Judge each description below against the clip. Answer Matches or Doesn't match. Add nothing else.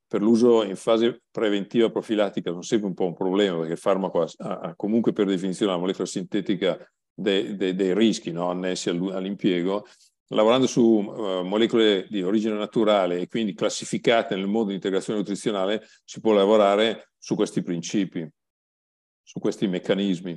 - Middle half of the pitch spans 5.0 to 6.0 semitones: Doesn't match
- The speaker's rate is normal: Matches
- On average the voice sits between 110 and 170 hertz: Doesn't match